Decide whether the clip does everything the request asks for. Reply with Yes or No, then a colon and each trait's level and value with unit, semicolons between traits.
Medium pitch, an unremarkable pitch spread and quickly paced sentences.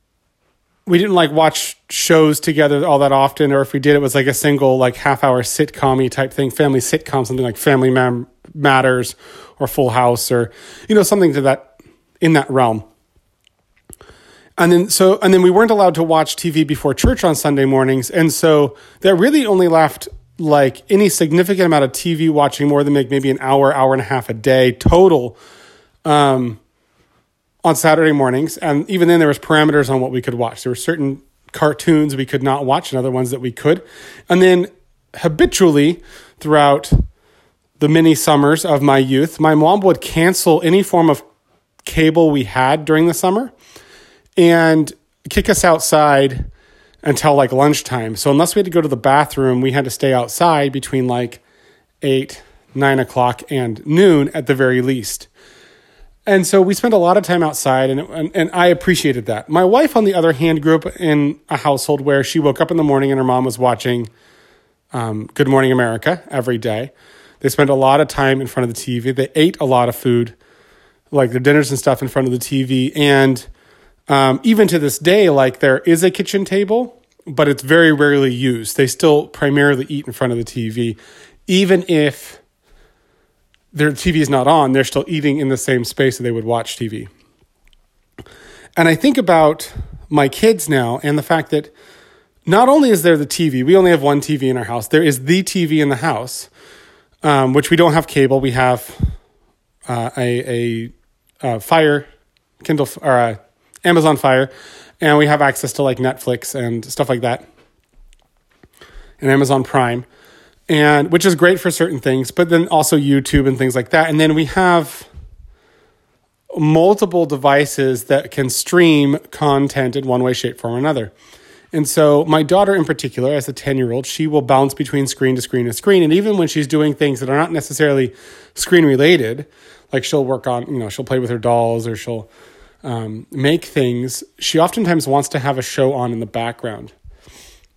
No: medium, 145 Hz; average, 3.7 semitones; average, 190 wpm